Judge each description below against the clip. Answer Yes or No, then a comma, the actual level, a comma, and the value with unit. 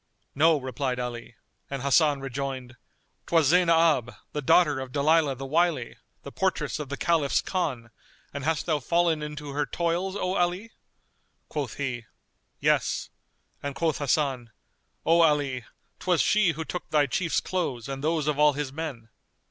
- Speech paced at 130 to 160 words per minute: Yes, average, 155 wpm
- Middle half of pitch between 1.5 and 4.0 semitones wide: Yes, average, 3.6 semitones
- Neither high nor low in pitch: Yes, medium, 150 Hz